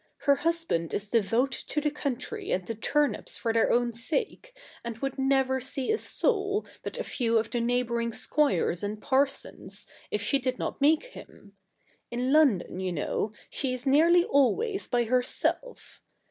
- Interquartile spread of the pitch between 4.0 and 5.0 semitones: Yes, average, 4.5 semitones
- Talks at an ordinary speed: Yes, average, 170 wpm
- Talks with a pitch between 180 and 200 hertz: No, very high, 265 Hz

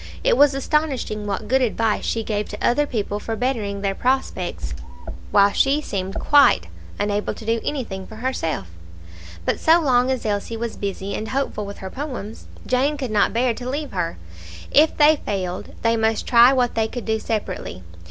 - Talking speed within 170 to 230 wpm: Yes, average, 180 wpm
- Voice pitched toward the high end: Yes, high, 225 Hz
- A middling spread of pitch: Yes, average, 4.5 semitones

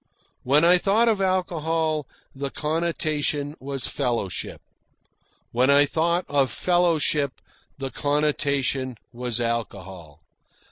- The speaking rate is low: Yes, slow, 100 wpm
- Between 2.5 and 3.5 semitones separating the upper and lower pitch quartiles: No, average, 4.2 semitones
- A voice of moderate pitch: Yes, medium, 145 Hz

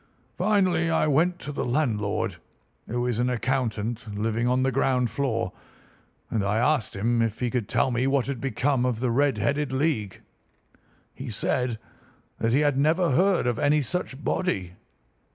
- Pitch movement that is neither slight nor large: Yes, average, 4.1 semitones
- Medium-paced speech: Yes, average, 170 wpm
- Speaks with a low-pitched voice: Yes, low, 125 Hz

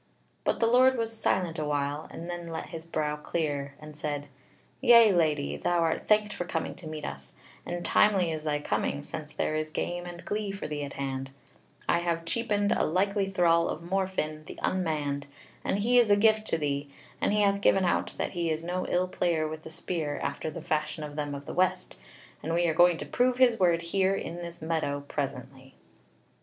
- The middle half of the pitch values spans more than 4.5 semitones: No, average, 4.0 semitones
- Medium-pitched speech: Yes, medium, 165 Hz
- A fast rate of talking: Yes, fast, 210 wpm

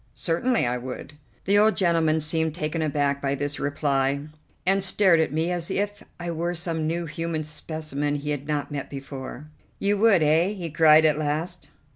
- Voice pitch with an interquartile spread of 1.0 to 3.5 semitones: Yes, average, 2.9 semitones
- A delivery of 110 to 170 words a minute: No, average, 180 wpm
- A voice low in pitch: No, medium, 155 Hz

